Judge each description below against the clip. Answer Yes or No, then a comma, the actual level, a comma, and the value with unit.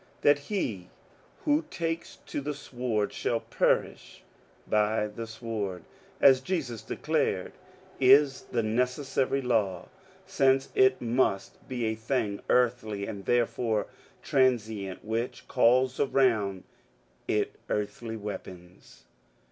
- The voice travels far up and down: No, average, 3.8 semitones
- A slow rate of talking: Yes, slow, 115 wpm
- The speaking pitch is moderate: No, low, 120 Hz